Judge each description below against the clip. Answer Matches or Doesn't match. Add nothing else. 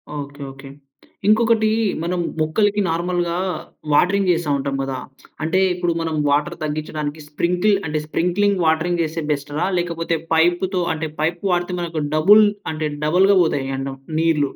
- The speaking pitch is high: Doesn't match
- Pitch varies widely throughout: Doesn't match